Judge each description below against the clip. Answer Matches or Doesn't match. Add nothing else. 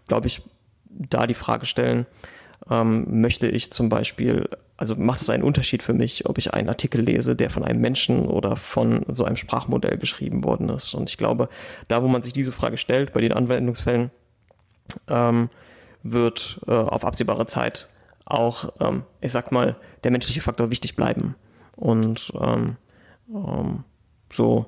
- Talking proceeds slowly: Doesn't match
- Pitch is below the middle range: Matches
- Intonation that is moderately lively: Doesn't match